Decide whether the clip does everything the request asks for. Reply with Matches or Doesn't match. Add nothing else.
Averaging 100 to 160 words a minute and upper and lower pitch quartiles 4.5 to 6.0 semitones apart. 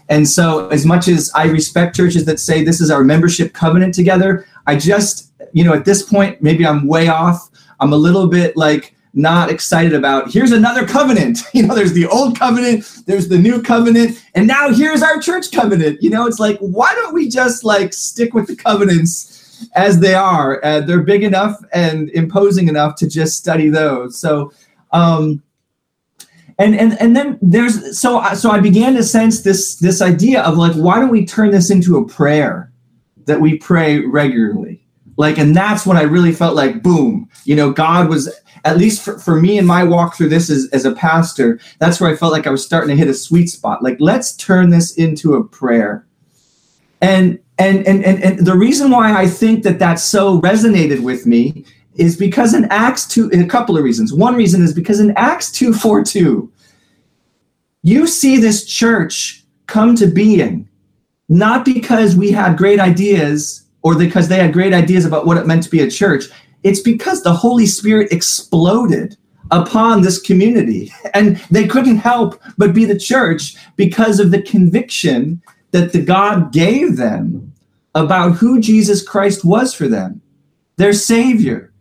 Doesn't match